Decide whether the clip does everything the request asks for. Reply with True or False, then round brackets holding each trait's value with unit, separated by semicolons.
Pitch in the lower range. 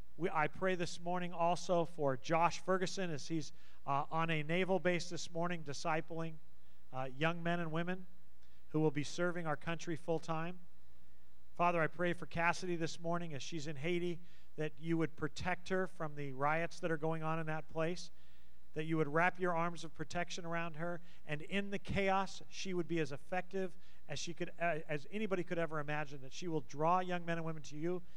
False (165 Hz)